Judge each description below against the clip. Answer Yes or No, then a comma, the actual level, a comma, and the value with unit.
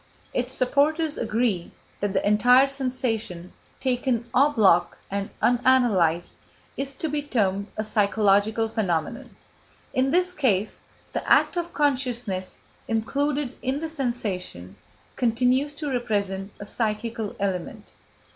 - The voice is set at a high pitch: Yes, high, 235 Hz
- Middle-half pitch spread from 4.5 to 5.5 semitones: Yes, average, 5.0 semitones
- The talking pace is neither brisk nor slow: No, slow, 120 wpm